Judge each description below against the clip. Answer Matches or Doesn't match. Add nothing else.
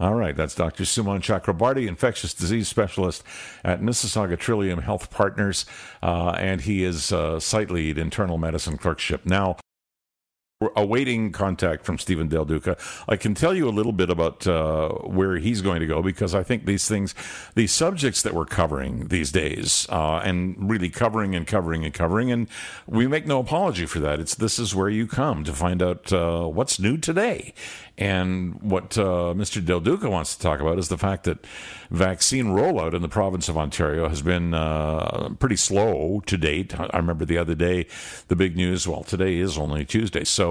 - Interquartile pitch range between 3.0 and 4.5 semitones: Matches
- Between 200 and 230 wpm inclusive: Doesn't match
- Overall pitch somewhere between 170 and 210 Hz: Doesn't match